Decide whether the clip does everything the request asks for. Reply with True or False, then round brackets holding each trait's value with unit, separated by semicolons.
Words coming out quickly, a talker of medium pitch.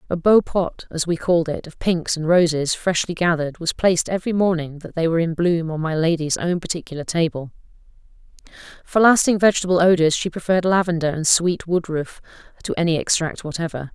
False (180 wpm; 170 Hz)